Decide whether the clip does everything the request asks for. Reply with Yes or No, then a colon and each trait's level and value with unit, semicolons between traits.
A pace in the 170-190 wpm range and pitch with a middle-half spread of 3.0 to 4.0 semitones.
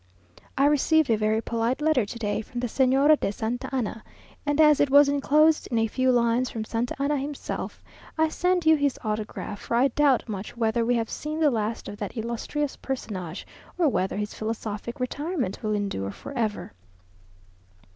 No: average, 180 wpm; average, 4.8 semitones